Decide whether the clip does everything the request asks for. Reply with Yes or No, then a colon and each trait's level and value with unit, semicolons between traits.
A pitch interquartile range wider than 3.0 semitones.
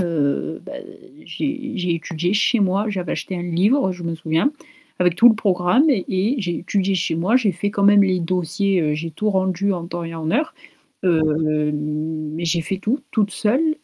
Yes: average, 3.6 semitones